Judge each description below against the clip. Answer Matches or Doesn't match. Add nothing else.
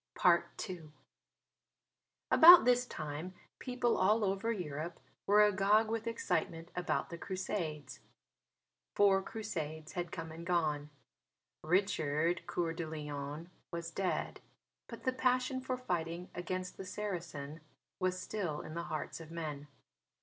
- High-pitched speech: Doesn't match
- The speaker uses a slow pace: Matches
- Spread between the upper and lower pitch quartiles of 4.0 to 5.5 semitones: Matches